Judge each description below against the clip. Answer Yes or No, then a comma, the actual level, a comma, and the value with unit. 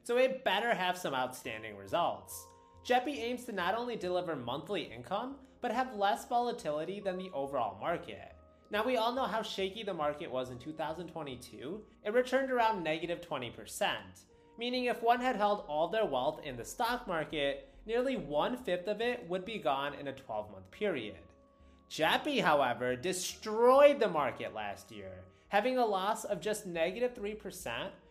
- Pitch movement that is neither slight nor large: No, wide, 8.8 semitones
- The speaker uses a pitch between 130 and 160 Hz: No, high, 190 Hz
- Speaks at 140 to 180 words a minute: Yes, average, 165 wpm